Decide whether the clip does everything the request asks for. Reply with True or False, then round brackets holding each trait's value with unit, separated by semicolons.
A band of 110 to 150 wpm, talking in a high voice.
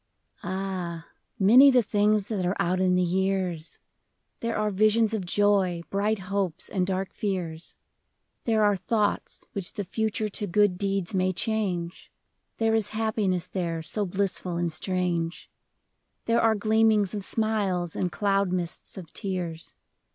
True (145 wpm; 195 Hz)